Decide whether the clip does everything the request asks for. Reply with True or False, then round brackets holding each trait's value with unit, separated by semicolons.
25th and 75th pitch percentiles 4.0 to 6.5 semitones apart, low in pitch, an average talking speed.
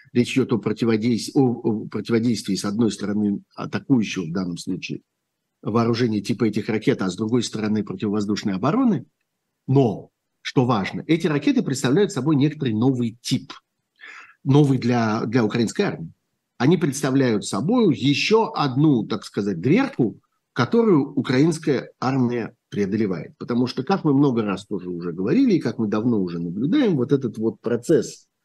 True (4.9 semitones; 120 Hz; 150 wpm)